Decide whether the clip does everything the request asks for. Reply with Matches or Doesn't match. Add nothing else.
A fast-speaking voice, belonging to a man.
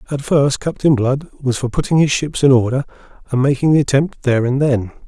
Matches